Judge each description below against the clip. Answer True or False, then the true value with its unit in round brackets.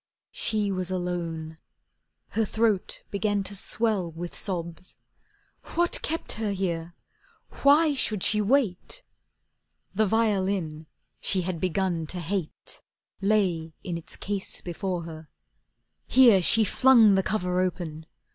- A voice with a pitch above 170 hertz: True (190 Hz)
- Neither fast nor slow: False (120 wpm)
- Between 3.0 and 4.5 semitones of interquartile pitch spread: True (4.0 semitones)